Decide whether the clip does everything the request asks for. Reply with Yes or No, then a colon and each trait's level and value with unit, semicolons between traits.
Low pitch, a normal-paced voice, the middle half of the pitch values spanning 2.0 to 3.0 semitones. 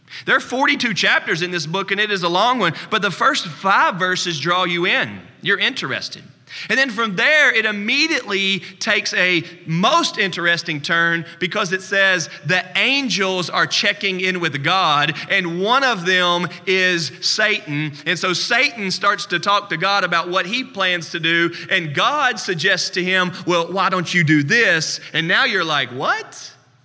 No: medium, 185 Hz; average, 180 wpm; average, 2.7 semitones